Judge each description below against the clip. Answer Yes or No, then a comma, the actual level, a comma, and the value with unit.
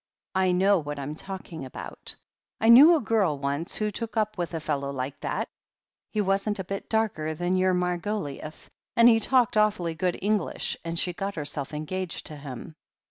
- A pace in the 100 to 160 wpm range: No, average, 185 wpm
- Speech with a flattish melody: No, wide, 5.4 semitones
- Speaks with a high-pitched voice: No, medium, 180 Hz